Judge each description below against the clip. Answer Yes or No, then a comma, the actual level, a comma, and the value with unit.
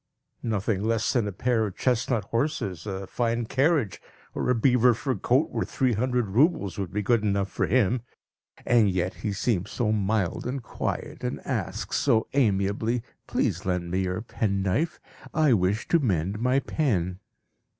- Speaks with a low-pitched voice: Yes, low, 110 Hz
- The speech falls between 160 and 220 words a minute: Yes, average, 165 wpm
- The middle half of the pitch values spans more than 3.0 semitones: Yes, average, 4.3 semitones